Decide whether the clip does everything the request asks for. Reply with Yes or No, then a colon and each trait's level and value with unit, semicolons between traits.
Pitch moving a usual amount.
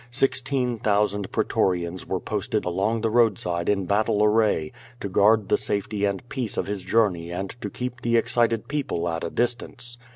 Yes: average, 3.8 semitones